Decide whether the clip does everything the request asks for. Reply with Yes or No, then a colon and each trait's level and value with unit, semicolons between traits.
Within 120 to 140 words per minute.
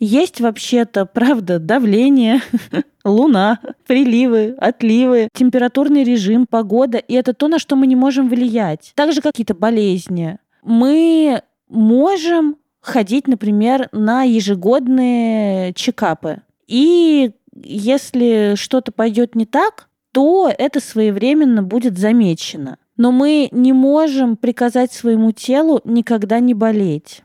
No: slow, 110 wpm